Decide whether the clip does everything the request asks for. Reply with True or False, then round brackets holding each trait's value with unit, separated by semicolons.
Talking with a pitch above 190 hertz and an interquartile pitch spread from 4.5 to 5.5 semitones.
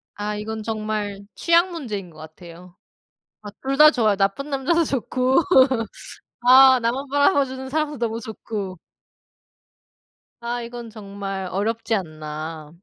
True (220 Hz; 5.1 semitones)